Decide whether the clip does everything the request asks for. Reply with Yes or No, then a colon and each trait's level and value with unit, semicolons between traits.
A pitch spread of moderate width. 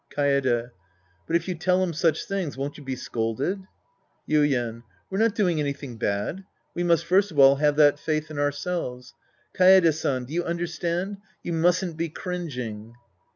Yes: average, 4.4 semitones